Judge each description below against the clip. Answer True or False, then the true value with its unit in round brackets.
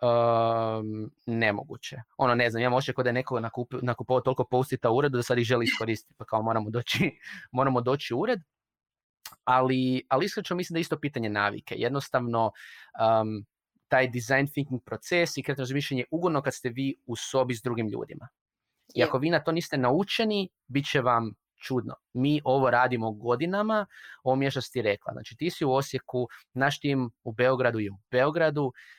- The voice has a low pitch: True (130 Hz)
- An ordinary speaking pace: False (180 wpm)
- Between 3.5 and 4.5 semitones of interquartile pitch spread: False (3.0 semitones)